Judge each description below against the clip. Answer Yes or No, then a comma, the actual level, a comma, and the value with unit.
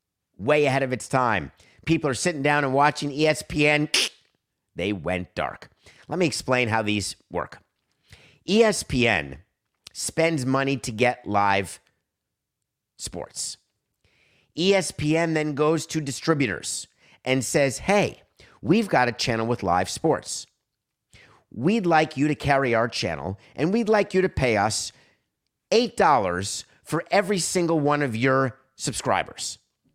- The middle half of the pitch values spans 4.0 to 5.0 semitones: No, wide, 5.6 semitones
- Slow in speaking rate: Yes, slow, 130 wpm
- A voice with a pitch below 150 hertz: Yes, medium, 140 Hz